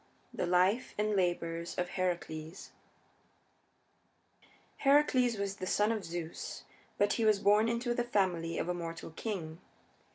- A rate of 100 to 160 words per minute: Yes, average, 140 wpm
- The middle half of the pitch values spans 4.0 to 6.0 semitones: Yes, average, 4.3 semitones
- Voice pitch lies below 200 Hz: Yes, high, 190 Hz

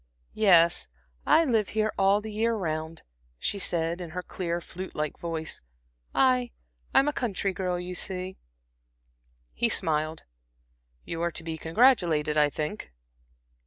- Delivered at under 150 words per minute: Yes, average, 140 wpm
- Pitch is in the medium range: Yes, medium, 180 Hz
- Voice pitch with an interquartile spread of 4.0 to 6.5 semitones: Yes, average, 4.5 semitones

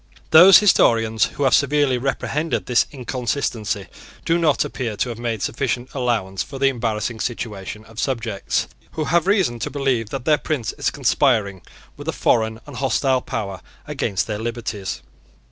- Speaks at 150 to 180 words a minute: Yes, average, 160 wpm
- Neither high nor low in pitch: No, low, 120 Hz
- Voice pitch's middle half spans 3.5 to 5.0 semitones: Yes, average, 3.9 semitones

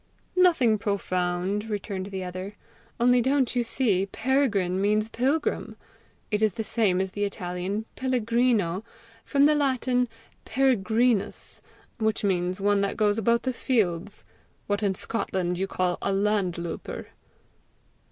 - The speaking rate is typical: No, slow, 130 wpm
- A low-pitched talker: No, high, 210 Hz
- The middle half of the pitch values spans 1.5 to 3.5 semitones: No, average, 4.2 semitones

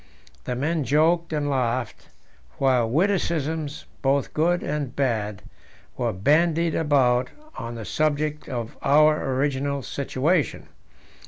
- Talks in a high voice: No, medium, 145 Hz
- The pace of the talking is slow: Yes, slow, 110 wpm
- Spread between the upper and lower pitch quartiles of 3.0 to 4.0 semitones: Yes, average, 3.3 semitones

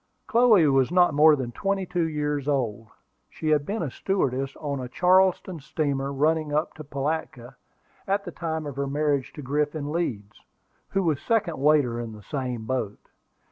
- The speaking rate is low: No, average, 175 wpm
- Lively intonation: No, average, 3.6 semitones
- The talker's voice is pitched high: No, medium, 150 Hz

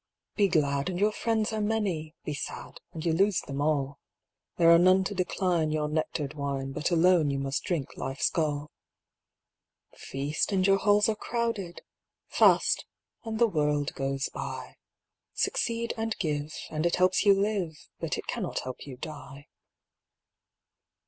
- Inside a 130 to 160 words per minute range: Yes, average, 155 wpm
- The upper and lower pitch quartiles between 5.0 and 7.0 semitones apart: Yes, wide, 5.4 semitones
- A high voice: No, medium, 165 Hz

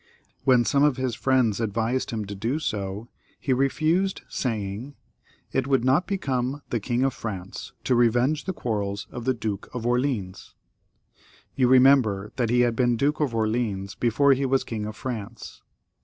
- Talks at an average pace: Yes, average, 170 wpm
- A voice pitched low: Yes, low, 120 Hz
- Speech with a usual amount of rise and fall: Yes, average, 3.6 semitones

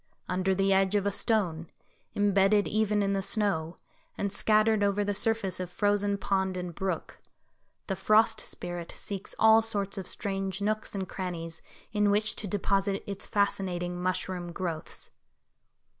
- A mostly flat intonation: Yes, narrow, 2.0 semitones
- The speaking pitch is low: No, high, 195 Hz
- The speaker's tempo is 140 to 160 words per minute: Yes, average, 150 wpm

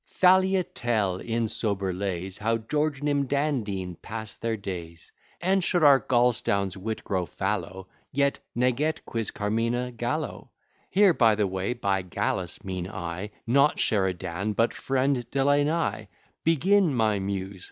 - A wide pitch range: Yes, wide, 6.4 semitones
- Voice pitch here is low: Yes, low, 115 Hz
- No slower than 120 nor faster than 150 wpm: Yes, average, 140 wpm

